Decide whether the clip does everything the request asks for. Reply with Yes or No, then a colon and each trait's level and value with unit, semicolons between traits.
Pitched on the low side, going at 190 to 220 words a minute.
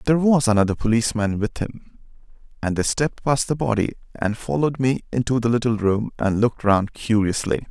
No: low, 115 Hz; average, 180 wpm